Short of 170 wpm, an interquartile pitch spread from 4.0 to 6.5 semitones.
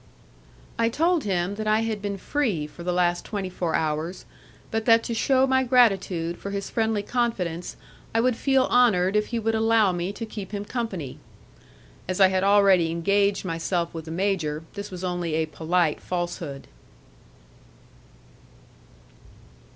Yes: average, 160 wpm; average, 4.4 semitones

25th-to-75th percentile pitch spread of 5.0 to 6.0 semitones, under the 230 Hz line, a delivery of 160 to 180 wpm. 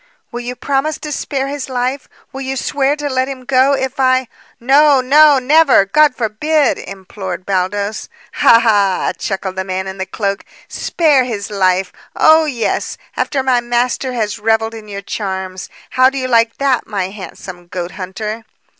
No: average, 5.3 semitones; high, 240 Hz; average, 170 wpm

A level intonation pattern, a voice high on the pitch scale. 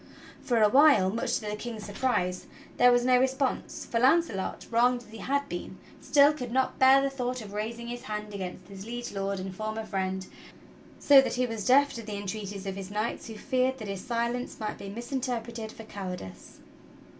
No: average, 3.9 semitones; high, 230 Hz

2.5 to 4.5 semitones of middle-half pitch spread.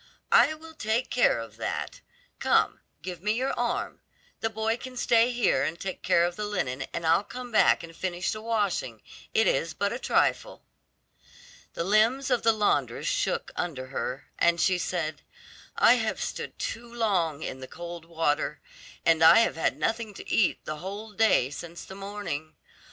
No: wide, 5.5 semitones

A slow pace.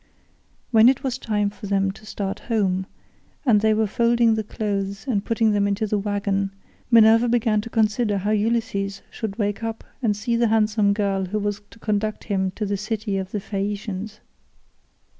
No: average, 180 wpm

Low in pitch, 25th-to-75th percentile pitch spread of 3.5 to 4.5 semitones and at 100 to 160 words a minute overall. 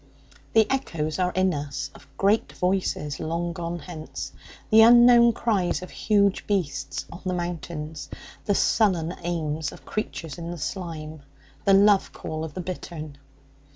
No: medium, 175 Hz; average, 3.9 semitones; average, 150 wpm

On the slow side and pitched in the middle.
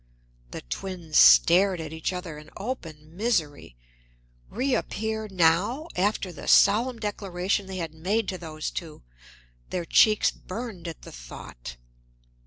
Yes: slow, 130 wpm; medium, 180 Hz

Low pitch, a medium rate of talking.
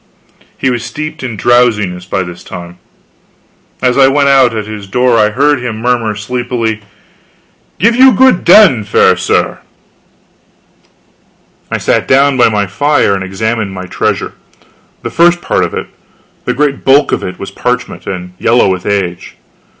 Yes: low, 120 Hz; average, 160 wpm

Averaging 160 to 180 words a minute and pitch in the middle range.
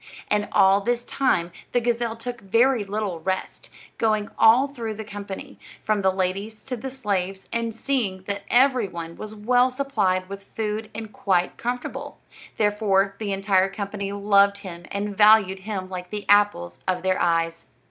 No: average, 165 wpm; high, 205 Hz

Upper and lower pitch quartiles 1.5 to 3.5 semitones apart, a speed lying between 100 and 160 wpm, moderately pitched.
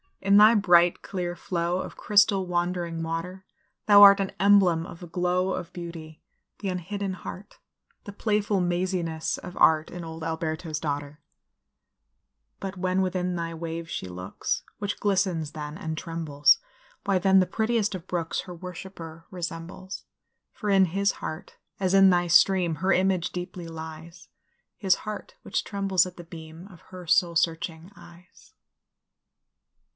Yes: narrow, 2.6 semitones; average, 150 wpm; medium, 180 Hz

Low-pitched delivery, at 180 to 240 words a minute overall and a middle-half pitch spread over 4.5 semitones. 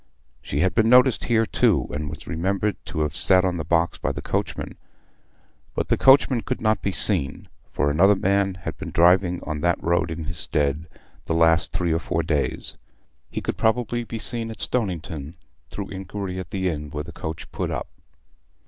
No: very low, 90 Hz; average, 195 wpm; average, 4.2 semitones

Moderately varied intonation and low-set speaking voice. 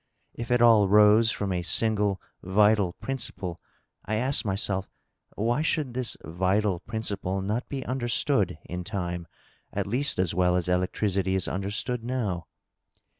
Yes: average, 4.1 semitones; low, 105 Hz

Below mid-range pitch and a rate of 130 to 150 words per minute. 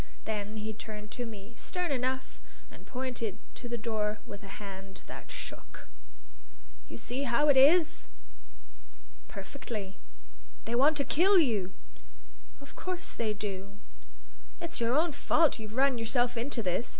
No: high, 235 Hz; average, 145 wpm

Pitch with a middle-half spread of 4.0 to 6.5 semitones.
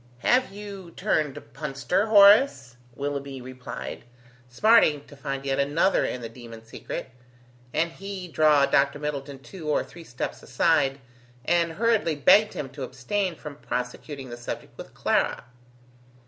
Yes: average, 4.8 semitones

